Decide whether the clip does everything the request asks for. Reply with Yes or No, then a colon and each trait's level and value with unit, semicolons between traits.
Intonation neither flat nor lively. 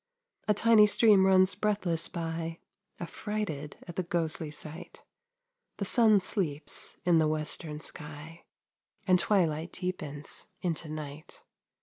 Yes: average, 3.8 semitones